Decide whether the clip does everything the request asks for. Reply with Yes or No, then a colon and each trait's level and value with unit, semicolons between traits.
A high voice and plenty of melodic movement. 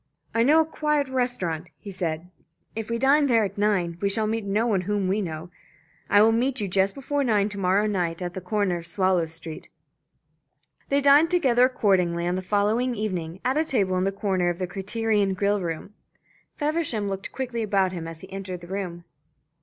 No: high, 200 Hz; average, 4.3 semitones